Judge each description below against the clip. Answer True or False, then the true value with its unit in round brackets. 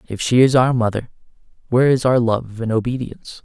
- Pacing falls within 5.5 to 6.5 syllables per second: True (6.0 syllables/s)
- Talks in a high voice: False (120 Hz)